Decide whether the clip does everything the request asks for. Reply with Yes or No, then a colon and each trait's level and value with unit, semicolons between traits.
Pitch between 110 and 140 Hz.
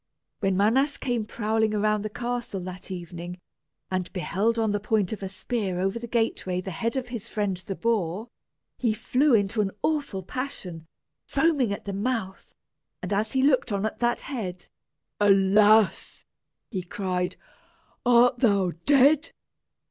No: high, 210 Hz